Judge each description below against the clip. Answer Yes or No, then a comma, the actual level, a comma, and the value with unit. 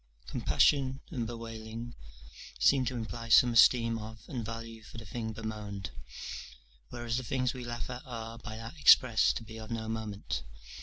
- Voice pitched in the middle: No, low, 115 Hz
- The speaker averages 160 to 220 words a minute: Yes, average, 165 wpm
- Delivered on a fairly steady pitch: Yes, narrow, 1.5 semitones